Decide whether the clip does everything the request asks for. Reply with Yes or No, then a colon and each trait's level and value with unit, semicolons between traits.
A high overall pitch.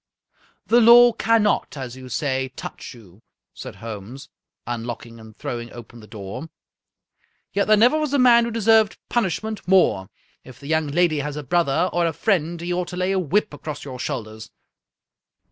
No: medium, 155 Hz